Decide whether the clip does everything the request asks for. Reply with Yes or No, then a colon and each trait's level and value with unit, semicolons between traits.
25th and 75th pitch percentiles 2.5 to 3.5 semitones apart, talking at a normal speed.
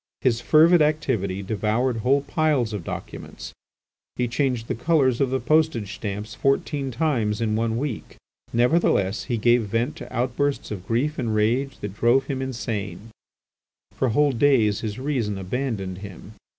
No: average, 4.3 semitones; average, 150 wpm